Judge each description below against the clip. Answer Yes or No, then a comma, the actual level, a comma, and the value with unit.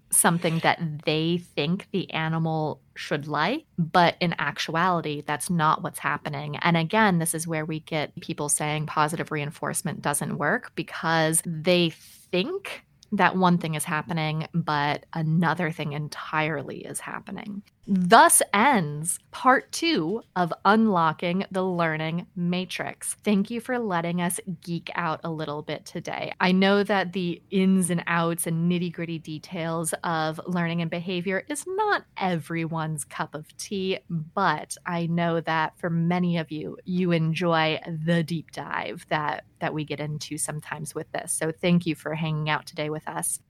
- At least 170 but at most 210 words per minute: No, average, 155 wpm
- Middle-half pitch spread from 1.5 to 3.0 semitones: Yes, average, 2.7 semitones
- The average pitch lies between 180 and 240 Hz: No, medium, 170 Hz